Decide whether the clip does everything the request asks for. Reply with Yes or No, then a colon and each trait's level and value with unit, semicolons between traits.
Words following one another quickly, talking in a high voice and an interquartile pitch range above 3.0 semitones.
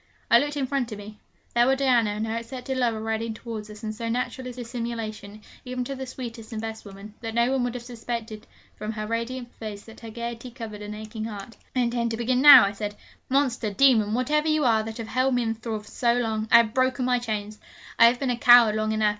No: fast, 240 wpm; high, 230 Hz; narrow, 2.5 semitones